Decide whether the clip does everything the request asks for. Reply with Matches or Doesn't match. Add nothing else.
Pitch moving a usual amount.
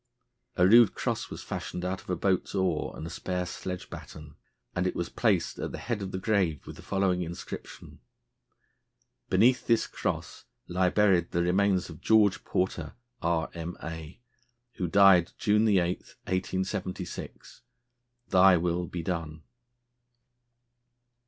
Doesn't match